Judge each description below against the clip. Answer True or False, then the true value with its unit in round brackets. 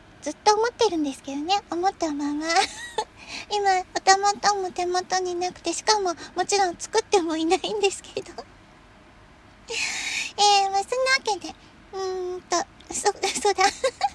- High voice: True (390 Hz)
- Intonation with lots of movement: False (2.4 semitones)